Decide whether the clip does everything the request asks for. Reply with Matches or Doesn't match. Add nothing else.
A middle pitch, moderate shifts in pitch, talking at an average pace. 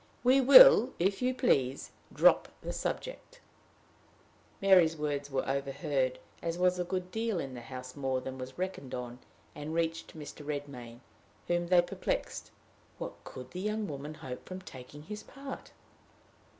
Doesn't match